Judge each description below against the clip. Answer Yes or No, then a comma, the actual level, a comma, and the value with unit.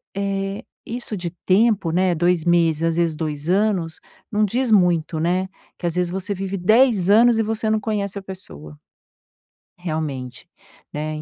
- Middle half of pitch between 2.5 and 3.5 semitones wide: No, average, 4.0 semitones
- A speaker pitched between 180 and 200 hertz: Yes, medium, 185 Hz